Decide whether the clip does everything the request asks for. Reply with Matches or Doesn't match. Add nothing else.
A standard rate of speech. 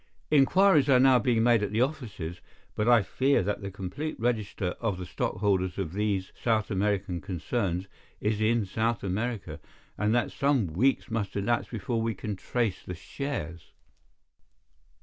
Matches